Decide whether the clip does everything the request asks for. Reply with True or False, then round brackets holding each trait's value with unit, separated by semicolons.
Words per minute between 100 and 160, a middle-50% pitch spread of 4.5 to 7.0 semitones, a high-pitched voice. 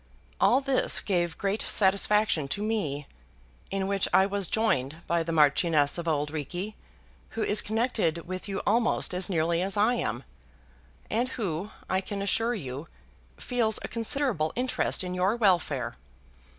True (150 wpm; 4.9 semitones; 195 Hz)